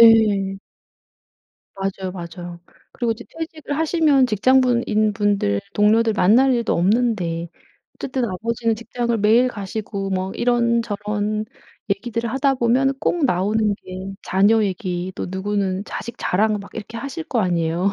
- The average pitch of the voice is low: No, high, 215 Hz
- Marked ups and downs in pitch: No, average, 3.6 semitones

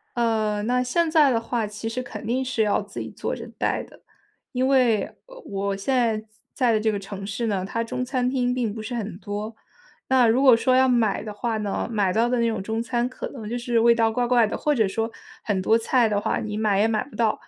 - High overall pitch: Yes, high, 230 Hz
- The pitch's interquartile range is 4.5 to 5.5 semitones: No, average, 2.8 semitones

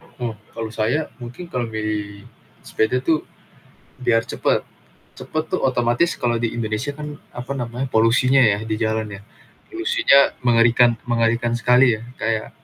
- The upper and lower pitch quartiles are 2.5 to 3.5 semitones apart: Yes, average, 2.9 semitones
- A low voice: Yes, low, 120 Hz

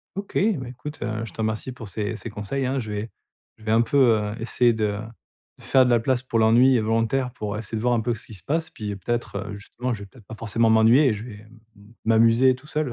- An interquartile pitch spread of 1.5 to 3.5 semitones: Yes, average, 2.8 semitones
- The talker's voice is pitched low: Yes, low, 115 Hz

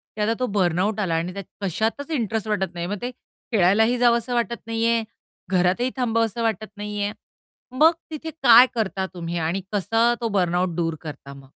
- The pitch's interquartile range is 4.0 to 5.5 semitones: Yes, average, 4.4 semitones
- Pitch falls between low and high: No, high, 210 Hz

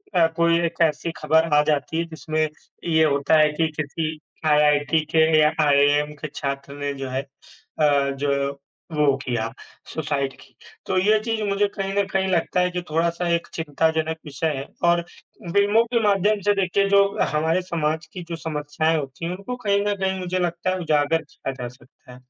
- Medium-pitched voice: Yes, medium, 160 Hz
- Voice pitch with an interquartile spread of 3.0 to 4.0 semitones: Yes, average, 3.7 semitones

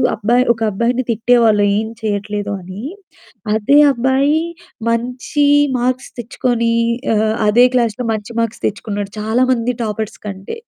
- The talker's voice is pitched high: Yes, high, 230 Hz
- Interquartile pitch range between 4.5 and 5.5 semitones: No, average, 2.9 semitones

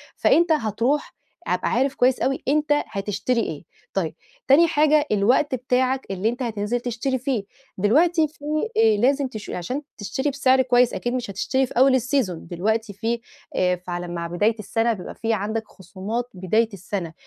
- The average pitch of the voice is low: No, high, 235 Hz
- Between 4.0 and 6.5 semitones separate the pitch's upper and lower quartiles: Yes, average, 4.6 semitones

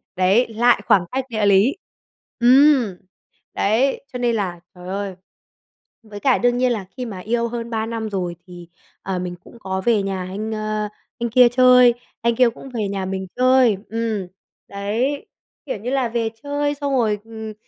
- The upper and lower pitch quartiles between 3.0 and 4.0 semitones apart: Yes, average, 3.7 semitones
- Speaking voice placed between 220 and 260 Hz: Yes, high, 225 Hz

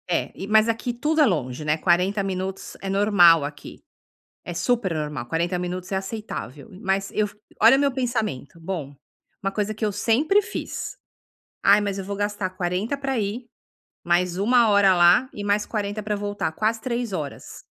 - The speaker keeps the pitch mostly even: No, average, 3.6 semitones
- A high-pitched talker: Yes, high, 200 Hz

